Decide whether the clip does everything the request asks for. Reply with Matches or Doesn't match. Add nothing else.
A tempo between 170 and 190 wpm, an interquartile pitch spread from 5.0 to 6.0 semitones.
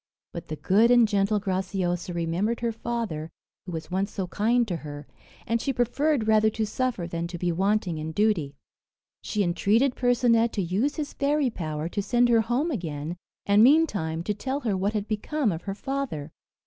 Matches